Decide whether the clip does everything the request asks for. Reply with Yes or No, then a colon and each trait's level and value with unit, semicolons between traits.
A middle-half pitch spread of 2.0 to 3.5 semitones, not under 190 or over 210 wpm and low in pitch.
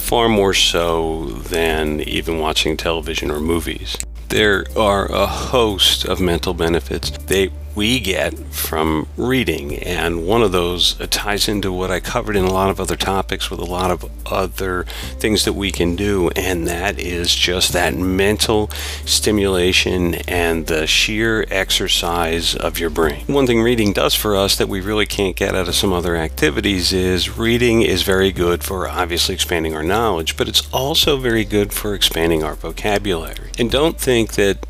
No: average, 3.2 semitones; average, 170 wpm; very low, 90 Hz